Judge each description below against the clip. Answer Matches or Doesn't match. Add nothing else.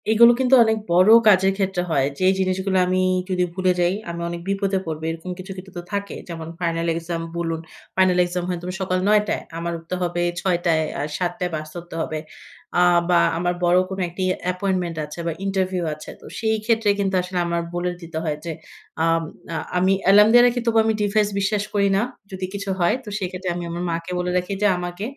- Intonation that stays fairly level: Matches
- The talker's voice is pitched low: Doesn't match